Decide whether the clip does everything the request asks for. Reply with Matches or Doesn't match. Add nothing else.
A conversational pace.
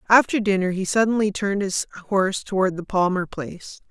Matches